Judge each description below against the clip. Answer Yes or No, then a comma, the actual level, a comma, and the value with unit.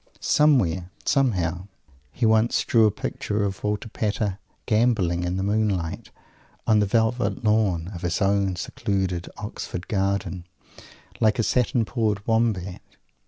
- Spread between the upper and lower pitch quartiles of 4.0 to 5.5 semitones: No, average, 3.4 semitones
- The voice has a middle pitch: No, low, 105 Hz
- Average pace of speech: No, slow, 130 wpm